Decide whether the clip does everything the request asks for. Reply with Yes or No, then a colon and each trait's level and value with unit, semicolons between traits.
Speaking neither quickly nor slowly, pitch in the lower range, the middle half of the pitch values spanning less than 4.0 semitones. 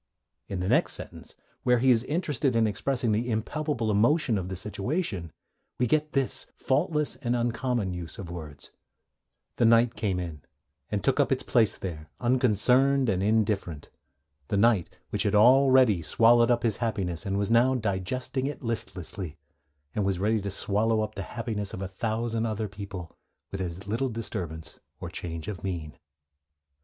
No: average, 165 wpm; low, 110 Hz; average, 4.3 semitones